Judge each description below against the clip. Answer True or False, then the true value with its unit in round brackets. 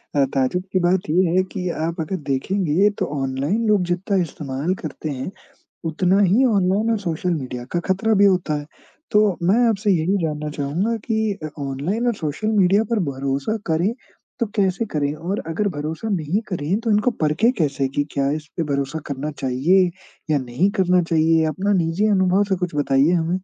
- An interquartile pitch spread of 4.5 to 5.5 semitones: True (4.9 semitones)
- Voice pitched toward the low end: False (175 Hz)